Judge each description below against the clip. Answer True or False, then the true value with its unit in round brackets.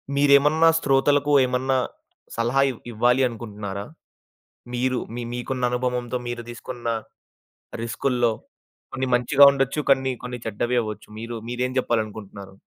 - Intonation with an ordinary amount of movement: False (2.3 semitones)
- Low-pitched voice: True (125 Hz)